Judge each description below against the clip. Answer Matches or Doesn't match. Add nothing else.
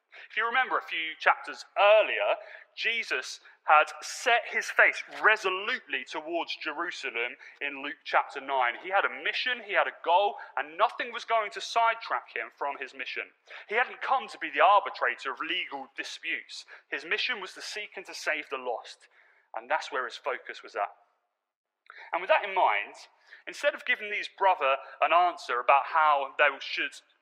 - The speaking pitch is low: Doesn't match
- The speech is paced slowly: Doesn't match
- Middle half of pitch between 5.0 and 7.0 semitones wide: Matches